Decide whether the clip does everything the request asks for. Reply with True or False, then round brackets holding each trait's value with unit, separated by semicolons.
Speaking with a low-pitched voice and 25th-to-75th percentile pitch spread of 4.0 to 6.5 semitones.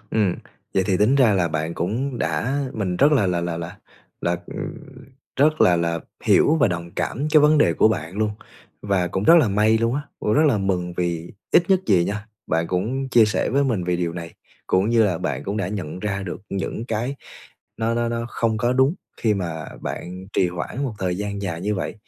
True (100 Hz; 4.9 semitones)